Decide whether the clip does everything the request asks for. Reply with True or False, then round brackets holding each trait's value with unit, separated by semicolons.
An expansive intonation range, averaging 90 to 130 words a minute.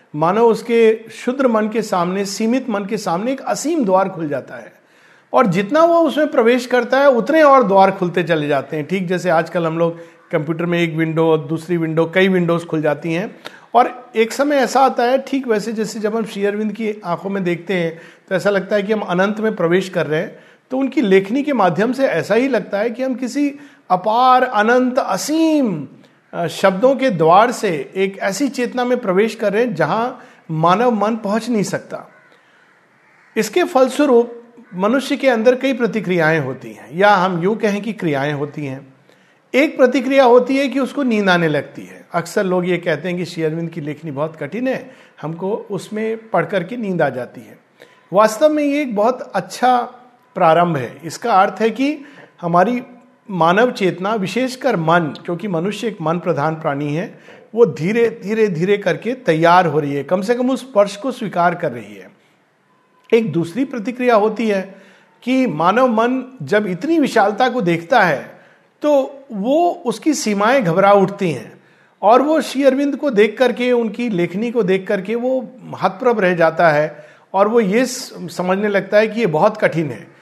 False (6.2 semitones; 185 wpm)